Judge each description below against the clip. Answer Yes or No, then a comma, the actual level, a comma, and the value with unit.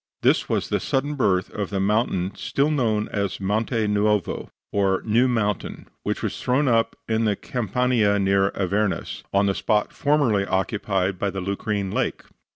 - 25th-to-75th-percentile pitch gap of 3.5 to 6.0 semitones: No, average, 2.8 semitones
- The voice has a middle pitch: No, low, 105 Hz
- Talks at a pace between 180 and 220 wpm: No, average, 160 wpm